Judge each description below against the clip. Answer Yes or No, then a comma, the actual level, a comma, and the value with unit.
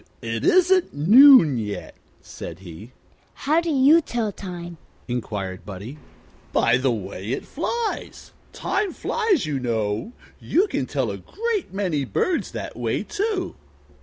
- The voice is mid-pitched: Yes, medium, 175 Hz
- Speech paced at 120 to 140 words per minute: Yes, slow, 135 wpm